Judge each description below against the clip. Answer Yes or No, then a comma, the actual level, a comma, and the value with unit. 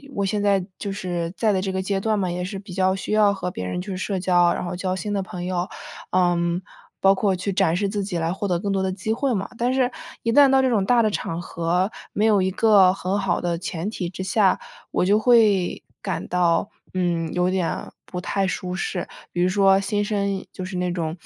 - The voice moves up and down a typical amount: No, narrow, 2.2 semitones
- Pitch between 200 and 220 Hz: No, high, 190 Hz